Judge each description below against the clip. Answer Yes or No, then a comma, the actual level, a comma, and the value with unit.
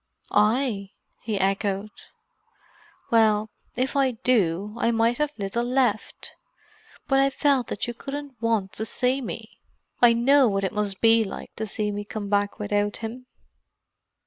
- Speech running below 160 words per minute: Yes, average, 150 wpm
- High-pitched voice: Yes, high, 225 Hz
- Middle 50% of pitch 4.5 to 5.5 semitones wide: No, average, 3.5 semitones